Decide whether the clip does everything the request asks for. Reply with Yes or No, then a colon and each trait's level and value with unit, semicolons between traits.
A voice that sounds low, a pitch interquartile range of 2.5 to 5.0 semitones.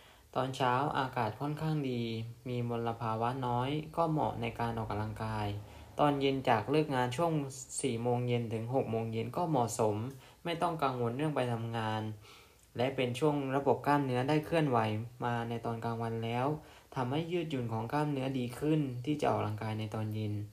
Yes: low, 120 Hz; average, 3.8 semitones